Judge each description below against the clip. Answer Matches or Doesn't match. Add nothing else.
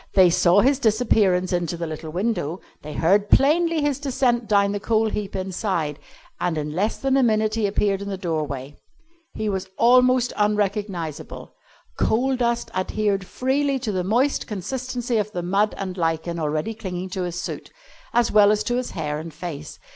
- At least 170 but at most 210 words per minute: Matches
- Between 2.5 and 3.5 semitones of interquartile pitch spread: Doesn't match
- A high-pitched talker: Matches